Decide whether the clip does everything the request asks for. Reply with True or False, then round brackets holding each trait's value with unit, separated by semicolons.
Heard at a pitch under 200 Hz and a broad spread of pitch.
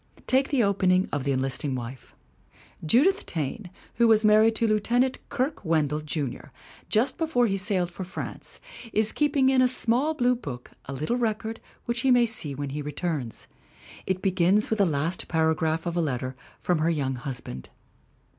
True (185 Hz; 8.0 semitones)